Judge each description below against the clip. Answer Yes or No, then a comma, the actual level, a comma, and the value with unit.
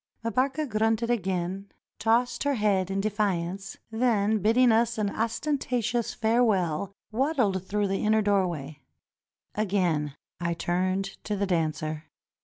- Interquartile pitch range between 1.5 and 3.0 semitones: No, average, 3.7 semitones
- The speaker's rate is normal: No, slow, 120 wpm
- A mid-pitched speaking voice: No, high, 205 Hz